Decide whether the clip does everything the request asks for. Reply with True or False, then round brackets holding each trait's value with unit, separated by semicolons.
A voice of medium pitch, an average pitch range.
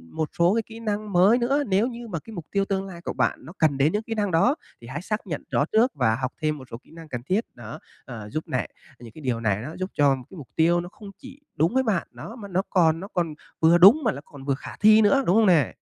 False (175 Hz; 6.7 semitones)